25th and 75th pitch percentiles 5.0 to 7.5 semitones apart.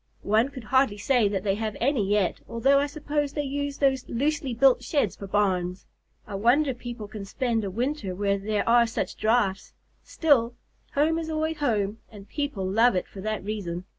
Yes: wide, 5.5 semitones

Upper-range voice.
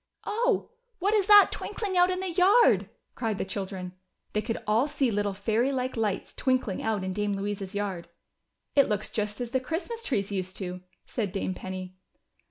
Yes: high, 215 Hz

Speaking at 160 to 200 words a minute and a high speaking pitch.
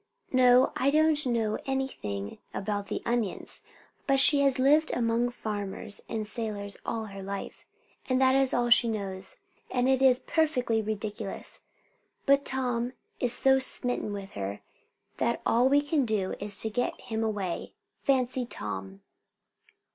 No: average, 145 wpm; high, 235 Hz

